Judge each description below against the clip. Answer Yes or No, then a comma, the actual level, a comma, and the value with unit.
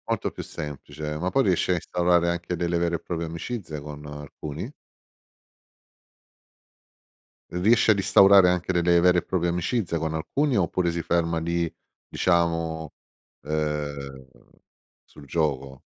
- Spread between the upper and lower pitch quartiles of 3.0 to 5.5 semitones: No, narrow, 2.6 semitones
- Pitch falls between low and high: No, very low, 85 Hz